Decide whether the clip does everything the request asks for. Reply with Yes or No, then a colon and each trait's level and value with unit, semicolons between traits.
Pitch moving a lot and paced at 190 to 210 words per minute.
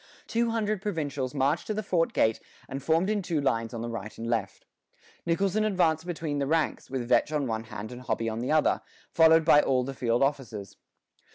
Yes: wide, 5.9 semitones; fast, 205 wpm